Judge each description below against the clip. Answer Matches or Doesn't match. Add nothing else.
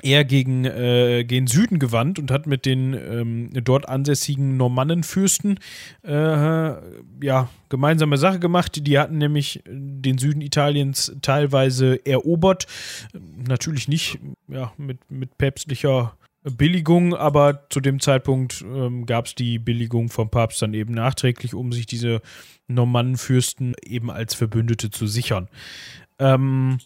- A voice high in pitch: Doesn't match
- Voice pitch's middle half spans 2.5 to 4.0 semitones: Matches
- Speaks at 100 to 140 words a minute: Matches